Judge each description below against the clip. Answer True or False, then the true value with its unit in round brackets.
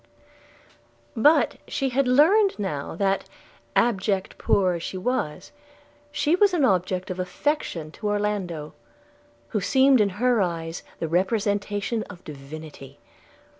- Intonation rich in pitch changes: True (6.2 semitones)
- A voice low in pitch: False (200 Hz)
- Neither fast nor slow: False (130 wpm)